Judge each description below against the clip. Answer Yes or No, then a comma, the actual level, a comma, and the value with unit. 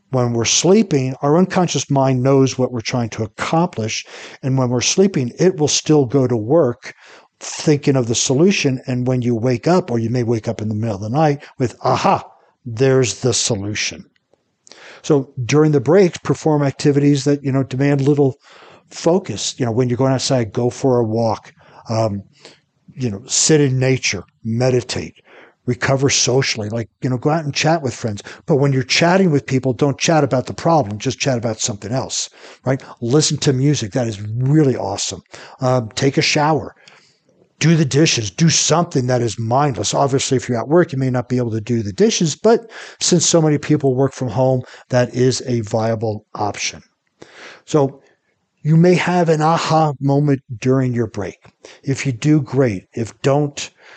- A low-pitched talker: Yes, low, 130 Hz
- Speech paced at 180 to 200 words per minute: Yes, average, 185 wpm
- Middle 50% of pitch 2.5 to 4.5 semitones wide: Yes, average, 3.5 semitones